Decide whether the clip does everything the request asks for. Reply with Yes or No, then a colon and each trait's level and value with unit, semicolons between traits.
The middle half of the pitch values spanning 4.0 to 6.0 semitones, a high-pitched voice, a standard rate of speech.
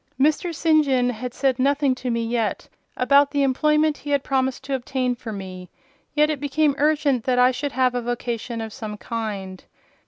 No: average, 3.3 semitones; very high, 255 Hz; average, 190 wpm